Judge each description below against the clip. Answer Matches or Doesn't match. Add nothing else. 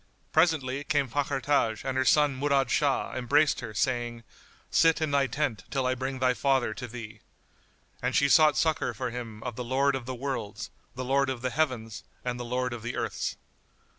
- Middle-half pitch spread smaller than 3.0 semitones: Matches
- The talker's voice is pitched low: Matches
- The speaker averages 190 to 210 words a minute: Matches